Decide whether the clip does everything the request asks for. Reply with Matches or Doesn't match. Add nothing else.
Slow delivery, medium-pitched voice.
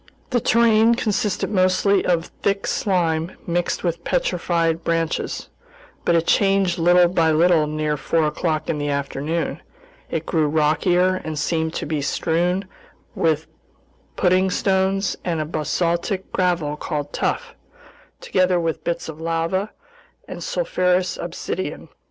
Matches